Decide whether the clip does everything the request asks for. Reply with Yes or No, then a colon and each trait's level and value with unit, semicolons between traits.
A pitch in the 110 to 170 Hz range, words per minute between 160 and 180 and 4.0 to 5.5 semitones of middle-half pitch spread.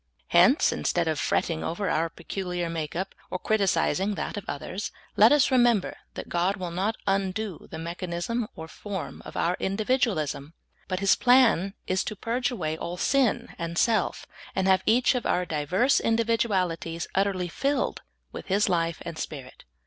No: high, 190 Hz; average, 165 wpm; average, 4.5 semitones